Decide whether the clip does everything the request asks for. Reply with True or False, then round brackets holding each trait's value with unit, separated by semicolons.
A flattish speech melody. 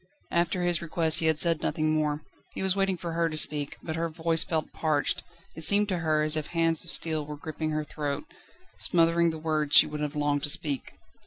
True (1.7 semitones)